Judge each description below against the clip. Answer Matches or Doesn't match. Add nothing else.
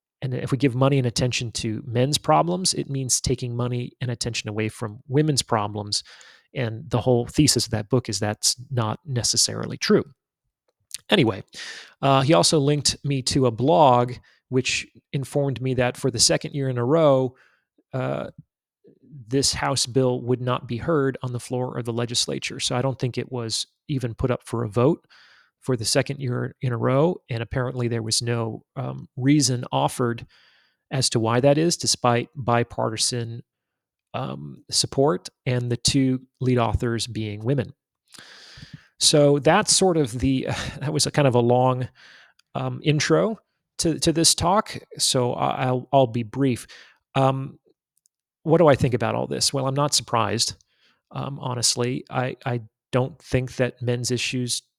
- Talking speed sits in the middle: Matches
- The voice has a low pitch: Matches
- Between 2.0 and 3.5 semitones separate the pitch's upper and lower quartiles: Matches